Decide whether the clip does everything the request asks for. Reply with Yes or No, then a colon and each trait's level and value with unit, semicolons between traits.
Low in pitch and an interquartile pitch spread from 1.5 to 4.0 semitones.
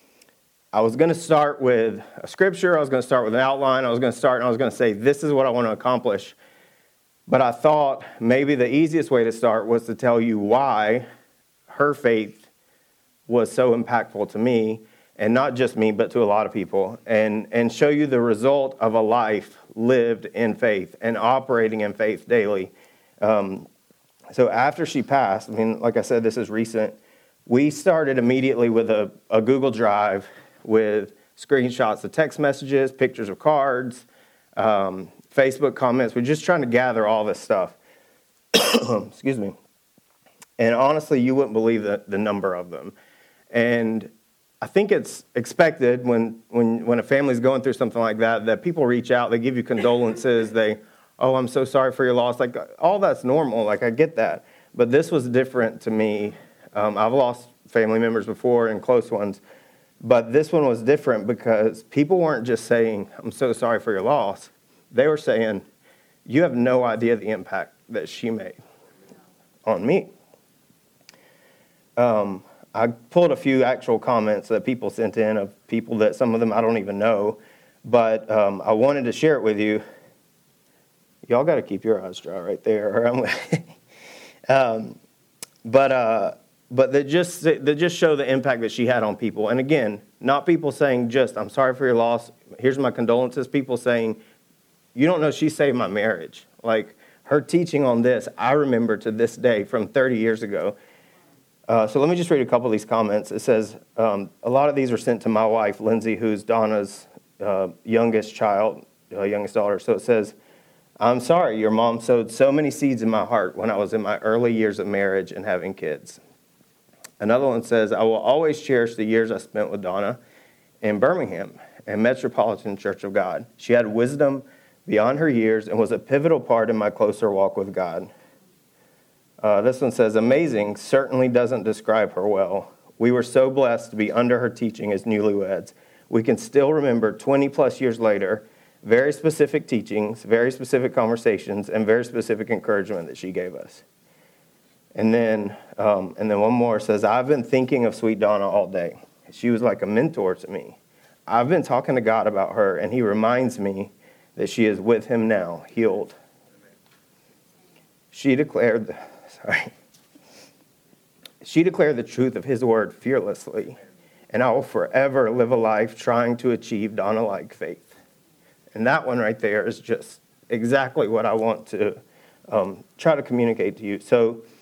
Yes: low, 115 Hz; average, 3.3 semitones